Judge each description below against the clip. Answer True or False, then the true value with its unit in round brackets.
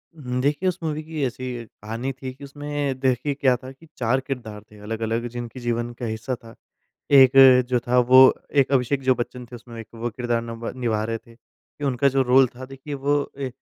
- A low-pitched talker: True (125 Hz)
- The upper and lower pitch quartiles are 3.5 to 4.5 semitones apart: False (2.4 semitones)